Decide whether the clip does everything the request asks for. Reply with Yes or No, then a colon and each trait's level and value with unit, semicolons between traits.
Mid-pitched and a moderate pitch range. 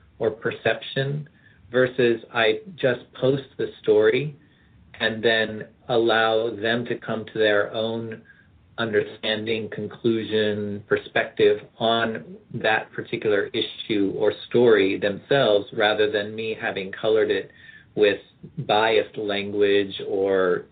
No: low, 115 Hz; average, 3.6 semitones